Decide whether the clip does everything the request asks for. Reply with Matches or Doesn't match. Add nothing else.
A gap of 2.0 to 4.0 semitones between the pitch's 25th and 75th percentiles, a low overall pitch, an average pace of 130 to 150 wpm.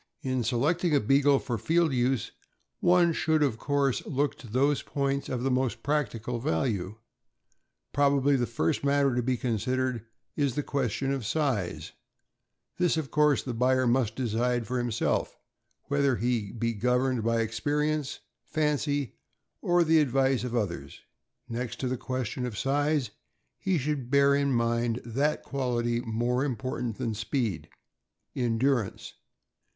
Matches